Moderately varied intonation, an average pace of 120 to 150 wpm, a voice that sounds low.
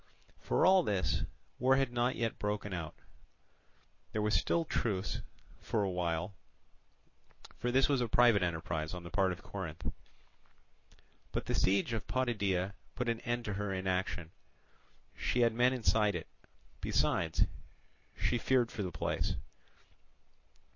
Yes: average, 4.8 semitones; average, 140 wpm; low, 105 Hz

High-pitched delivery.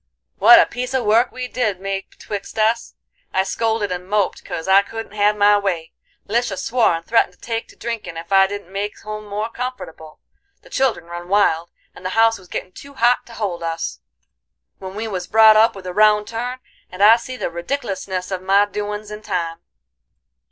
Yes: high, 205 Hz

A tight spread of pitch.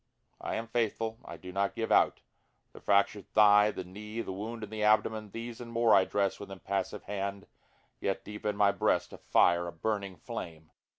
Yes: narrow, 2.1 semitones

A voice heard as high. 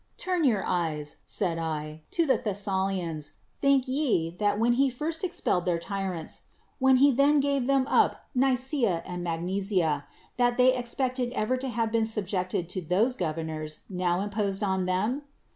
Yes: high, 205 Hz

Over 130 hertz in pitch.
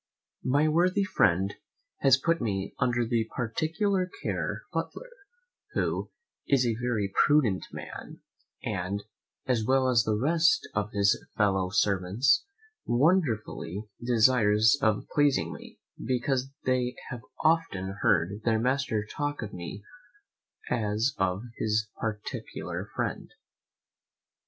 No: low, 115 Hz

